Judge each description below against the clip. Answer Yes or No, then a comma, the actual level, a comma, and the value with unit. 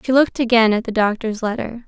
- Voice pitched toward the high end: Yes, high, 230 Hz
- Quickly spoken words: Yes, fast, 225 wpm